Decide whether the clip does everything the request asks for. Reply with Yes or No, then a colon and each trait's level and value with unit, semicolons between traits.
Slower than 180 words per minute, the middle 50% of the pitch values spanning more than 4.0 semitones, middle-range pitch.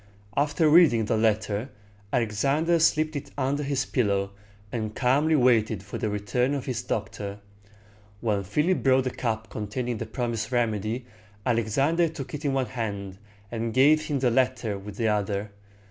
No: average, 160 wpm; average, 4.4 semitones; low, 120 Hz